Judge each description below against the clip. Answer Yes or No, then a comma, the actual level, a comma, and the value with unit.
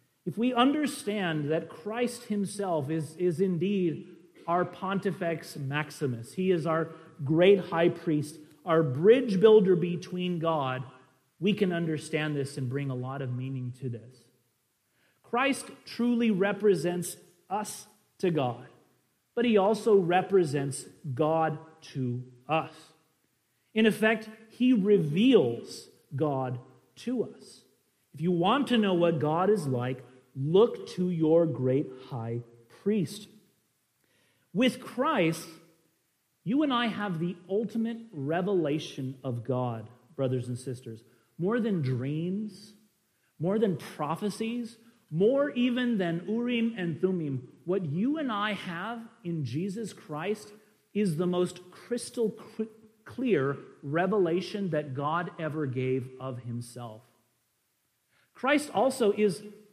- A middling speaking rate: No, slow, 120 wpm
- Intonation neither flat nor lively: No, wide, 7.1 semitones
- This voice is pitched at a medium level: Yes, medium, 170 Hz